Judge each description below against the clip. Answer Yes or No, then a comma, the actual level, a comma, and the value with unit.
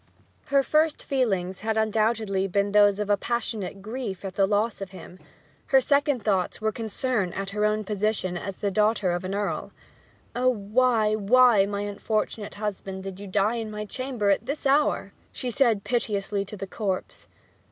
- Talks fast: No, average, 175 wpm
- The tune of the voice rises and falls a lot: No, average, 2.9 semitones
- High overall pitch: Yes, high, 210 Hz